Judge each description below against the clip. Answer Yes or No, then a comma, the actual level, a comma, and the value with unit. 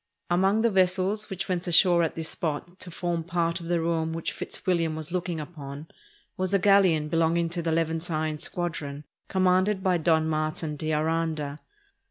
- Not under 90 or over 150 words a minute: No, average, 175 wpm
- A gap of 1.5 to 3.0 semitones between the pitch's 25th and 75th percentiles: Yes, narrow, 2.4 semitones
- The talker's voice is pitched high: No, medium, 170 Hz